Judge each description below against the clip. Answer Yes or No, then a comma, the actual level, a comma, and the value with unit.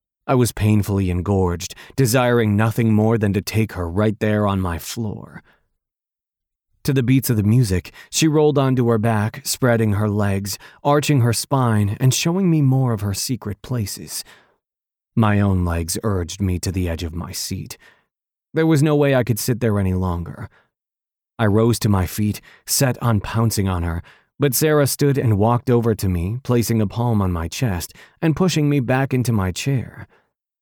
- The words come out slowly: No, average, 180 wpm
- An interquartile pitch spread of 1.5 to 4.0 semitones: No, average, 4.6 semitones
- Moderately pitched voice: No, low, 110 Hz